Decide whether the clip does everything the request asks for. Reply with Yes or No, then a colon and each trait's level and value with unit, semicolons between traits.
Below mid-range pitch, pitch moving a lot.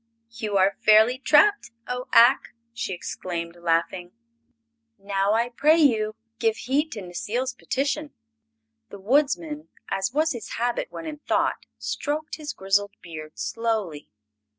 No: high, 225 Hz; wide, 6.1 semitones